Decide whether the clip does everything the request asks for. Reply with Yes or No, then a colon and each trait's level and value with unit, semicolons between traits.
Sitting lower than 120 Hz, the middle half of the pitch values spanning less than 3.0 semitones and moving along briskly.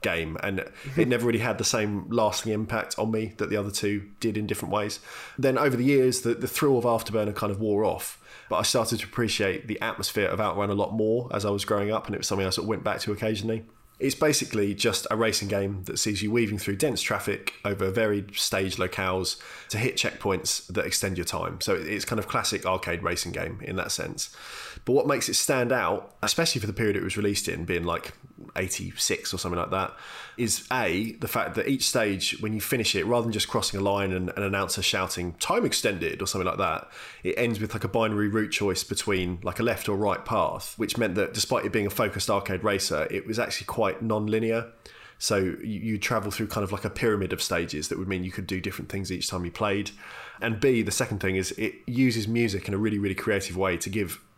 Yes: low, 105 Hz; narrow, 2.6 semitones; fast, 235 wpm